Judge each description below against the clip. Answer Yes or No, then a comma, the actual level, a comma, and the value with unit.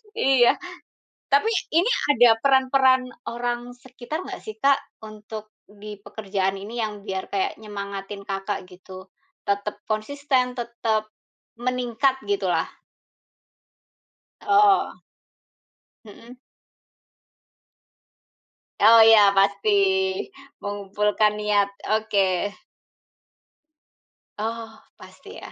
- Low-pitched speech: No, high, 220 Hz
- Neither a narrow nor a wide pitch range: Yes, average, 3.7 semitones